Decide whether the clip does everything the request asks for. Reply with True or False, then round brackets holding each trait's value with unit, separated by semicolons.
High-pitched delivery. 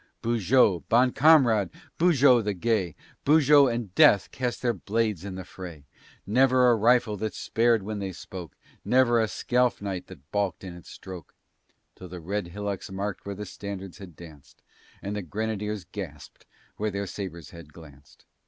False (100 Hz)